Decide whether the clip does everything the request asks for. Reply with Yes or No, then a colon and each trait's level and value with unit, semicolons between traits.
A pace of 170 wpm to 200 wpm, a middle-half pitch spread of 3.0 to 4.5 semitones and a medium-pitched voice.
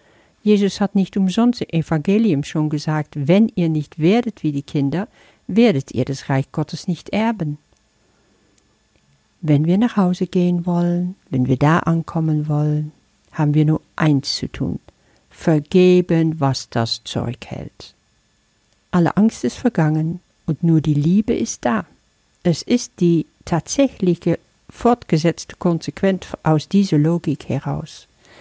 No: average, 135 wpm; average, 3.6 semitones; medium, 165 Hz